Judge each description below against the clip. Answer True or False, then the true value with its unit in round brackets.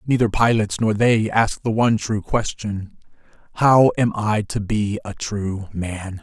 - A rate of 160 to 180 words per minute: True (165 wpm)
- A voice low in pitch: True (105 Hz)